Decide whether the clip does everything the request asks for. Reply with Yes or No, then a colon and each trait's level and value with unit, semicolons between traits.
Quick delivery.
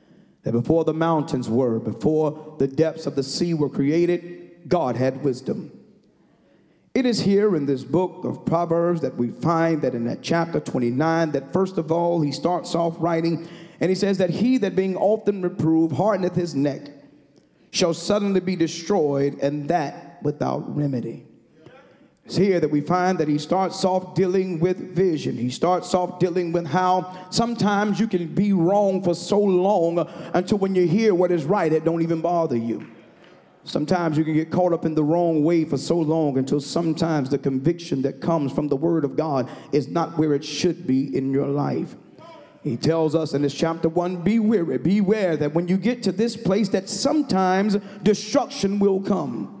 No: average, 185 wpm